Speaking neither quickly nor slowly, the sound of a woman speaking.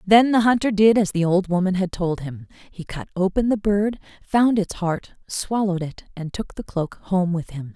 No: fast, 215 wpm; female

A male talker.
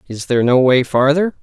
Yes: male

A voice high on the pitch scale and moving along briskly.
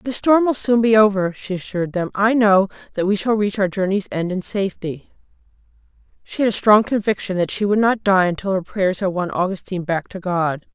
Yes: high, 195 Hz; fast, 220 wpm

